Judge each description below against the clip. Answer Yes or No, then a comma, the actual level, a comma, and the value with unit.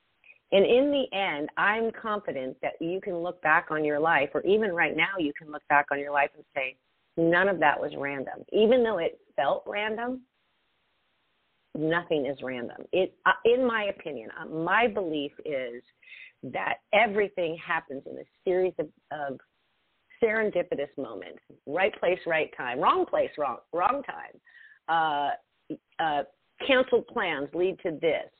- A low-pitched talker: No, medium, 180 Hz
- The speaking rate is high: No, average, 160 wpm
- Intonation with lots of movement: Yes, wide, 7.7 semitones